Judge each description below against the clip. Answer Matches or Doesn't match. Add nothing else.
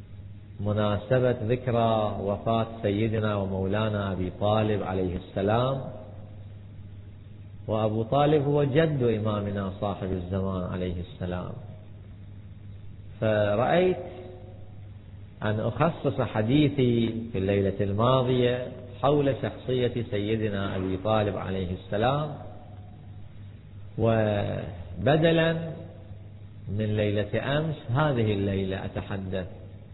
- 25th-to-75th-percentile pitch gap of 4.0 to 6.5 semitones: Doesn't match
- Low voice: Matches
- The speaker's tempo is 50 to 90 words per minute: Matches